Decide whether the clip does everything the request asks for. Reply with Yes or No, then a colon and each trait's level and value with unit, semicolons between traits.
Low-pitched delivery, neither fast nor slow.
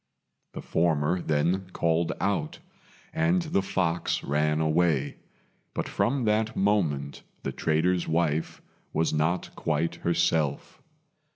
No: very low, 85 Hz; slow, 110 wpm